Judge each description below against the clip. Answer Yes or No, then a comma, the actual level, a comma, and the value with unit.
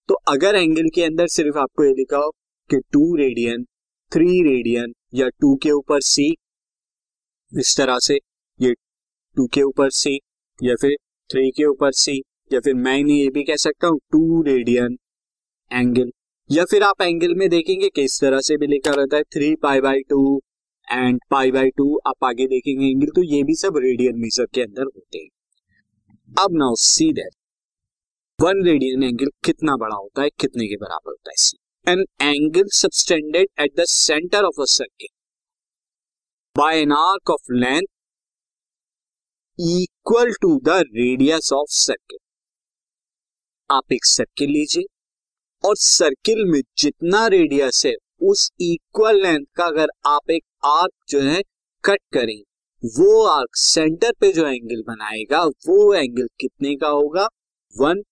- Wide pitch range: Yes, wide, 6.4 semitones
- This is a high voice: No, medium, 145 Hz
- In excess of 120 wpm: Yes, average, 160 wpm